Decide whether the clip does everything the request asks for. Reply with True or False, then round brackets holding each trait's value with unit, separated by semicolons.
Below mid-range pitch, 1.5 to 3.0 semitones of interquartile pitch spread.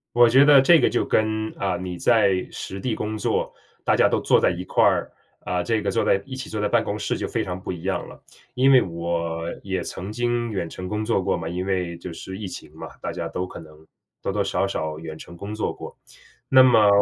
False (95 Hz; 3.7 semitones)